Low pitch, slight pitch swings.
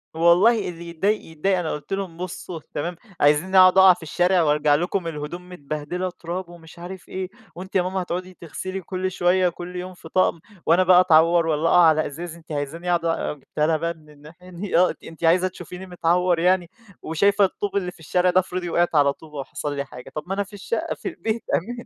No: medium, 175 Hz; narrow, 2.3 semitones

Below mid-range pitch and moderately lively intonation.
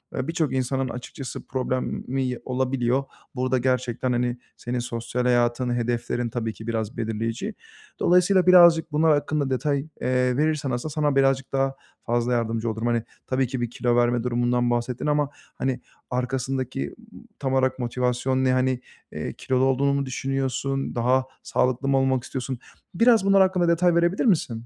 No: low, 130 Hz; narrow, 2.2 semitones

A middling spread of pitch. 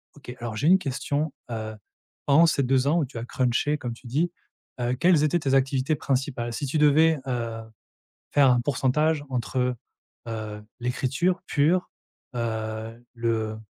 Yes: average, 4.0 semitones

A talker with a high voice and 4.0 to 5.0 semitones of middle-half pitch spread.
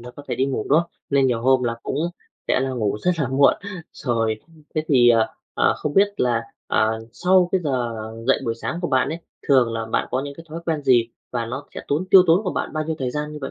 No: low, 135 Hz; average, 4.4 semitones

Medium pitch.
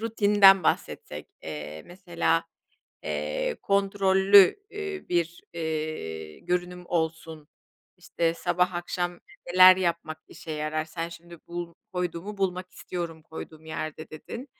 Yes: medium, 175 Hz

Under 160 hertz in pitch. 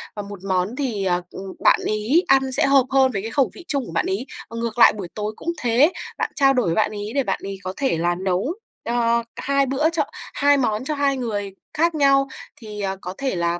No: high, 235 Hz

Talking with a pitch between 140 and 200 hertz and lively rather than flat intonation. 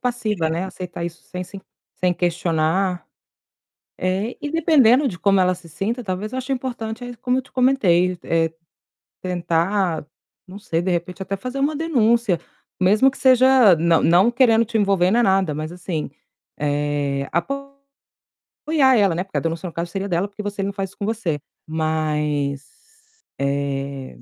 Yes: high, 190 Hz; wide, 6.1 semitones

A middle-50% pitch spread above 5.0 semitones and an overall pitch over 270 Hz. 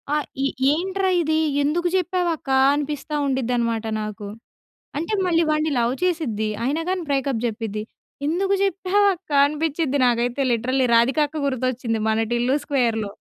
Yes: wide, 5.6 semitones; very high, 280 Hz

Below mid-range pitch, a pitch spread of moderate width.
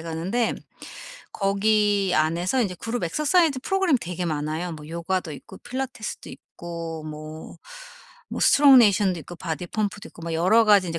No: medium, 185 Hz; average, 5.0 semitones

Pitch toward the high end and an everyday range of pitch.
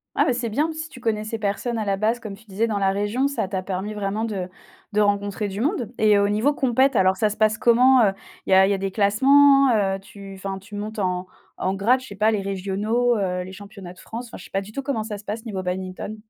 Yes: high, 210 Hz; average, 3.0 semitones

